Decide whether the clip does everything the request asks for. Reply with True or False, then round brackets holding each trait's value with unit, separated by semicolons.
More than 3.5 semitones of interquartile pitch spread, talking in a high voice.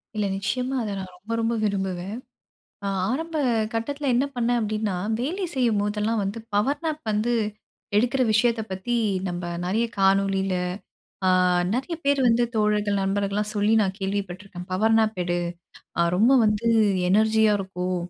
False (3.2 semitones; 210 Hz)